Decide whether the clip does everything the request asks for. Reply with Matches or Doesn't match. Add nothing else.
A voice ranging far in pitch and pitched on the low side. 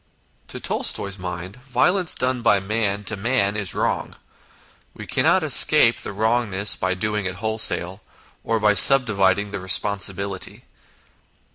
Doesn't match